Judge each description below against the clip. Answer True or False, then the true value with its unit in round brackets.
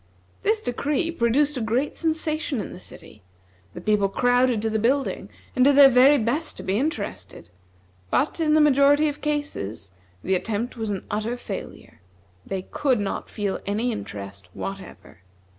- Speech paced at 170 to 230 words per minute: False (160 wpm)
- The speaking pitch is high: True (245 Hz)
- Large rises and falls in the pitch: True (6.2 semitones)